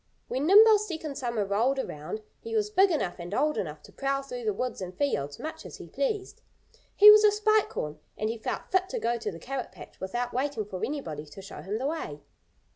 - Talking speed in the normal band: No, fast, 225 wpm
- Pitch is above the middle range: Yes, very high, 255 Hz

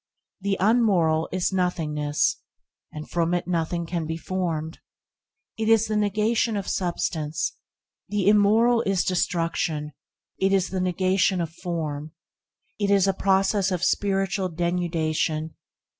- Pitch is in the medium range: Yes, medium, 180 Hz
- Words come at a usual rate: No, slow, 130 wpm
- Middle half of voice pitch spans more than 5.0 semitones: No, average, 3.3 semitones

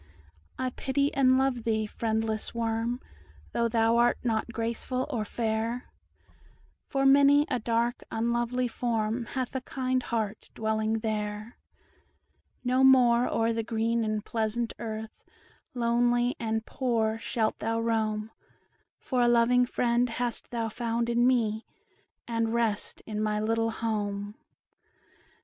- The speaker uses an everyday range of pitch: No, narrow, 1.8 semitones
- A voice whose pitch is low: No, high, 230 Hz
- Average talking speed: No, slow, 130 wpm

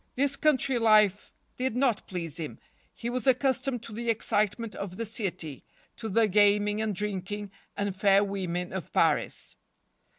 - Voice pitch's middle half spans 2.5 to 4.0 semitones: Yes, average, 3.3 semitones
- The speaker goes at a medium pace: Yes, average, 155 wpm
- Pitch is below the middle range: No, high, 210 Hz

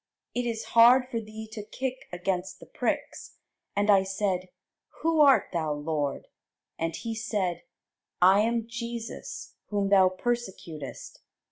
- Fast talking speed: No, slow, 135 wpm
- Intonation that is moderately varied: Yes, average, 4.3 semitones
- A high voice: Yes, high, 210 Hz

